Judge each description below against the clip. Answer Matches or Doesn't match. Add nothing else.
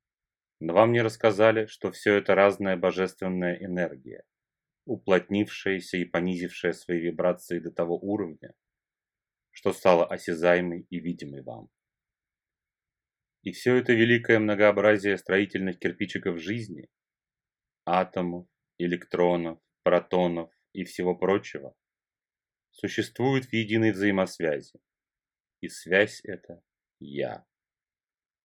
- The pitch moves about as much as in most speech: Matches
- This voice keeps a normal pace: Doesn't match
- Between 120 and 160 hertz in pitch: Doesn't match